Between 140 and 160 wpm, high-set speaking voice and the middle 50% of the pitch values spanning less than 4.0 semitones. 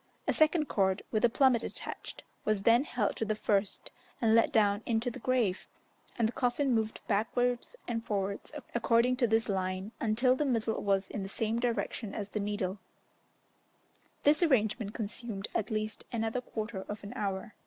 No: average, 175 wpm; high, 220 Hz; average, 2.9 semitones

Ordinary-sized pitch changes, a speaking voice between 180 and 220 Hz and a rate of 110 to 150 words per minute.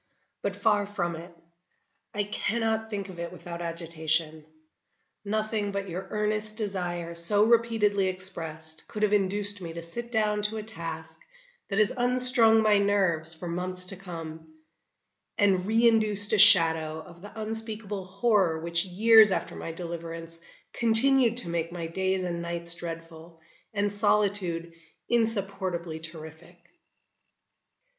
Yes: average, 4.0 semitones; high, 190 Hz; slow, 135 wpm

